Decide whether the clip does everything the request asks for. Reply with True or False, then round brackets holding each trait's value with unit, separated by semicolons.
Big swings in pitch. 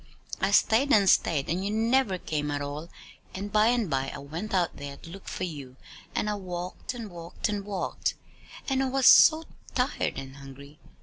True (6.8 semitones)